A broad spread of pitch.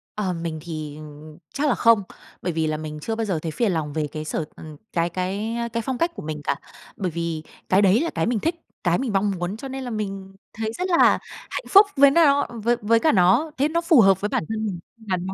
Yes: wide, 6.3 semitones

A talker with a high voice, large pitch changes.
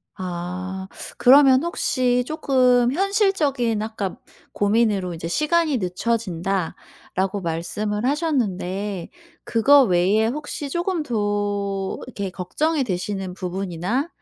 Yes: high, 210 Hz; wide, 6.3 semitones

